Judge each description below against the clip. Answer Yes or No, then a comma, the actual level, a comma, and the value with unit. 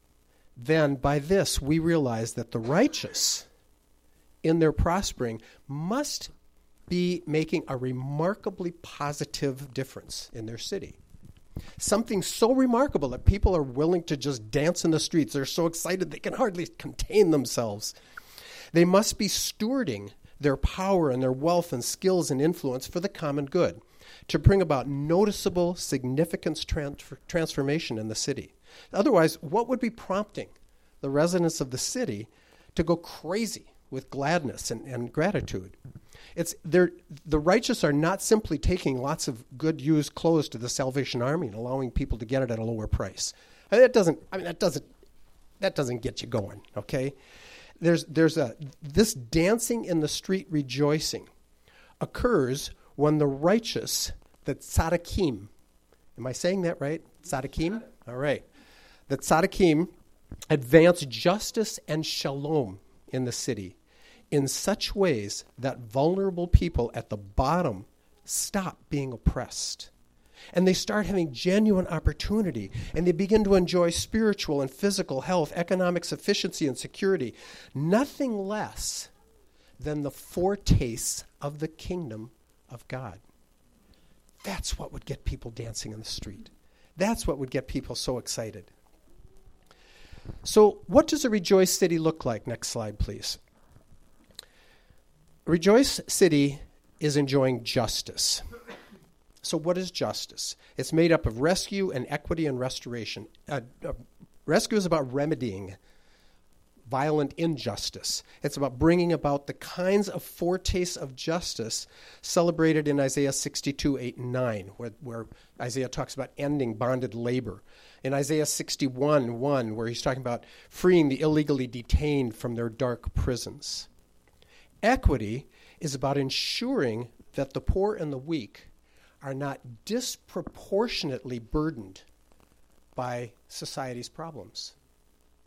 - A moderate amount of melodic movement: No, wide, 6.4 semitones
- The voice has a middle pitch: Yes, medium, 145 Hz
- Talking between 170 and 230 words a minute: No, slow, 135 wpm